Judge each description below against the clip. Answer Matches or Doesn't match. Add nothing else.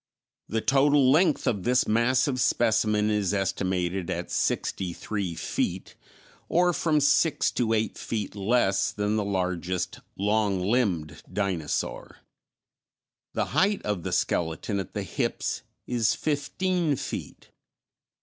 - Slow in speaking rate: Matches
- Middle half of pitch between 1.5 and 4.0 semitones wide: Doesn't match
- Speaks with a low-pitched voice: Matches